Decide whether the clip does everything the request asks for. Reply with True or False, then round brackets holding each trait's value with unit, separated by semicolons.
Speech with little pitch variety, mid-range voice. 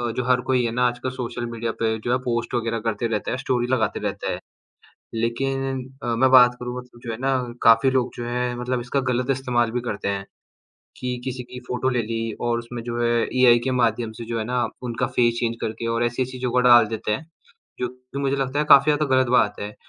False (1.5 semitones; 120 Hz)